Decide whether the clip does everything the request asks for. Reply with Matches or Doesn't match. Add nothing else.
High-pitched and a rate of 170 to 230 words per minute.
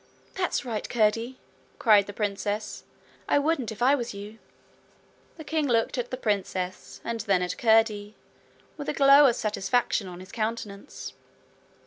Doesn't match